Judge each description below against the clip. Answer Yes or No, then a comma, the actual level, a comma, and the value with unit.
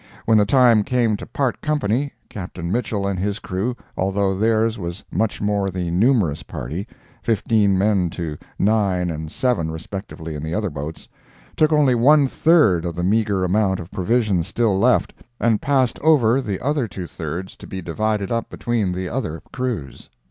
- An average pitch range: Yes, average, 4.5 semitones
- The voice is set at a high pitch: No, low, 100 Hz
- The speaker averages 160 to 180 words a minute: Yes, average, 170 wpm